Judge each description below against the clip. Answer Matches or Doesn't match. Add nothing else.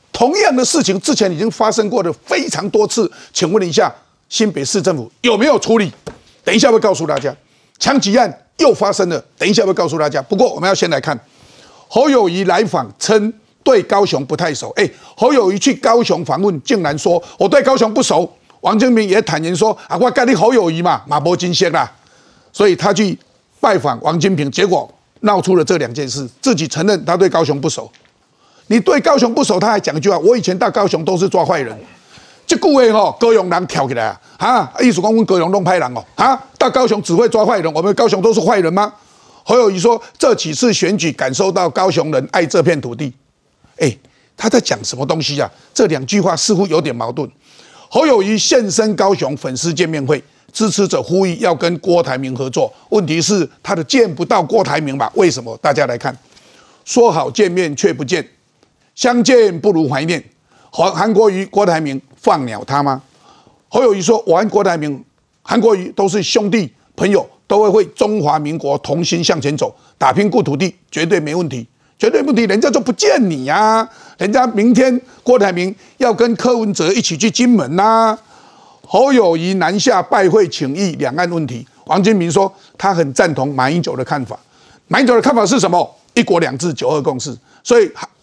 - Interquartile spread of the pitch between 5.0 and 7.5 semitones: Matches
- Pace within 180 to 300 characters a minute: Matches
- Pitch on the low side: Doesn't match